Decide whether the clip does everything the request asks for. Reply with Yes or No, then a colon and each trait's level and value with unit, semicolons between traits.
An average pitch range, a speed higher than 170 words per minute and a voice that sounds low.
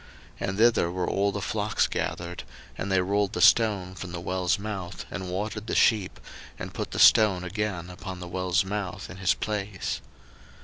No: narrow, 2.3 semitones; average, 185 wpm; very low, 95 Hz